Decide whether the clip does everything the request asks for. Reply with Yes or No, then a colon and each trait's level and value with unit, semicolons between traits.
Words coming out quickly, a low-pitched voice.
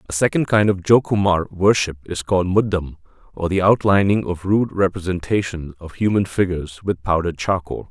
No: average, 160 wpm; very low, 95 Hz